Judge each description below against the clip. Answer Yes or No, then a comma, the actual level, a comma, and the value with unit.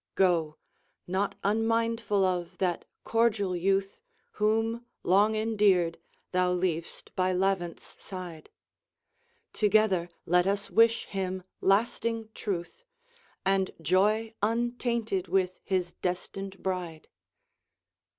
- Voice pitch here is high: Yes, high, 195 Hz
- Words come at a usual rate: No, slow, 95 wpm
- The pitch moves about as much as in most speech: Yes, average, 3.2 semitones